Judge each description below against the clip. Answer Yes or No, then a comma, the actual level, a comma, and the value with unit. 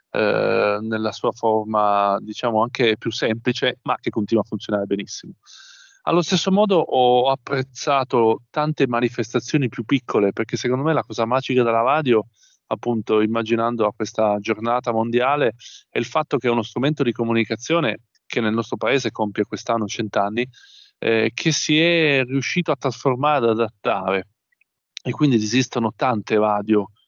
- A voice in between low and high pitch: No, low, 120 Hz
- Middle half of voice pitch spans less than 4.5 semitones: Yes, average, 3.7 semitones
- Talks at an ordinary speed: Yes, average, 150 wpm